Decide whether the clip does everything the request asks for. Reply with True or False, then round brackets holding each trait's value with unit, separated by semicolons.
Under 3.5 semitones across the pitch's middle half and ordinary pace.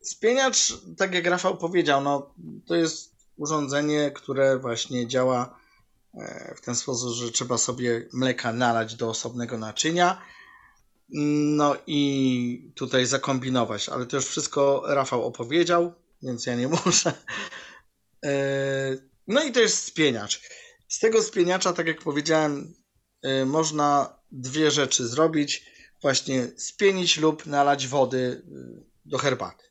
False (4.2 semitones; 120 wpm)